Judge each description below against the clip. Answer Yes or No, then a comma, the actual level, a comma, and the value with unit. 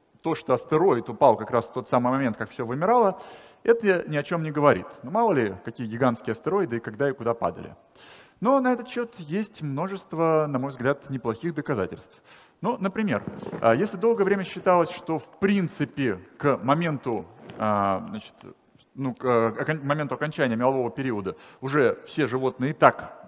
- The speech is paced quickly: Yes, fast, 165 wpm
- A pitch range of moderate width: No, wide, 7.1 semitones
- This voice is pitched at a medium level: Yes, medium, 145 Hz